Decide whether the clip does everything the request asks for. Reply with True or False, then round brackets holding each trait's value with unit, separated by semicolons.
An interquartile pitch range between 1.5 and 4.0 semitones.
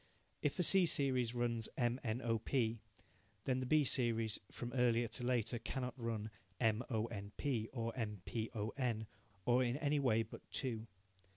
True (2.4 semitones)